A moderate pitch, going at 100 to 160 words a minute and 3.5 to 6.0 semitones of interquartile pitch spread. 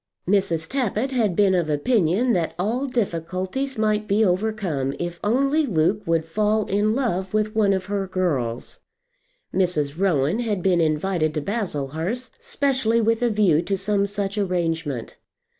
No: high, 195 Hz; average, 150 wpm; average, 4.7 semitones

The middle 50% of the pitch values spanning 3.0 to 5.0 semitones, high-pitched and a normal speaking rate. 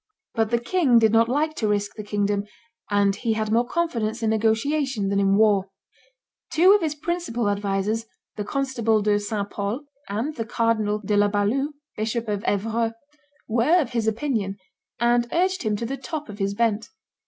Yes: average, 3.3 semitones; high, 225 Hz; average, 180 wpm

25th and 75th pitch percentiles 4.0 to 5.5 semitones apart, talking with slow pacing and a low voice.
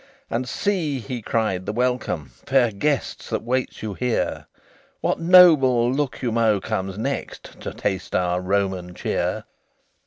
Yes: average, 5.0 semitones; slow, 130 wpm; low, 120 Hz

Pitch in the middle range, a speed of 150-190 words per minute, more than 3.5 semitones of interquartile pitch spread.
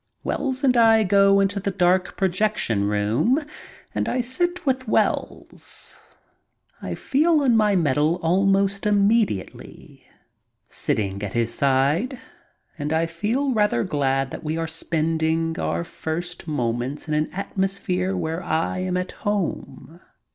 No: medium, 180 Hz; slow, 135 wpm; wide, 5.4 semitones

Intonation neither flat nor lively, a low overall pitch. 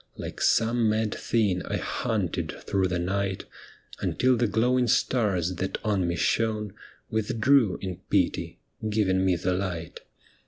Yes: average, 3.4 semitones; low, 105 Hz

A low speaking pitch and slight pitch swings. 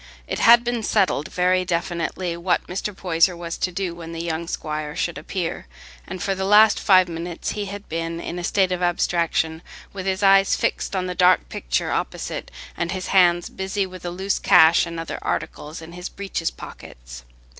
No: medium, 180 Hz; narrow, 2.3 semitones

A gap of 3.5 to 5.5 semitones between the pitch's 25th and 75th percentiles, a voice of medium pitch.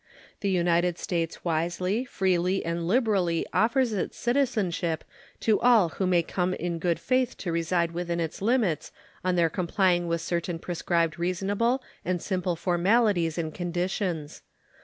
No: average, 2.9 semitones; medium, 180 Hz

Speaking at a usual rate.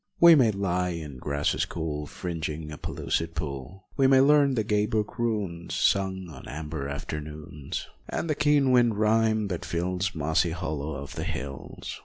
Yes: average, 165 wpm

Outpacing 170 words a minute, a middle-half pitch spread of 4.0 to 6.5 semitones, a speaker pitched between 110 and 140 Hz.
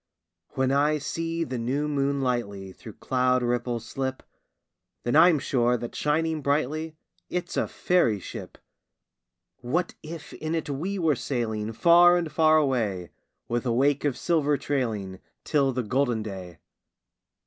No: average, 145 wpm; average, 4.7 semitones; low, 135 Hz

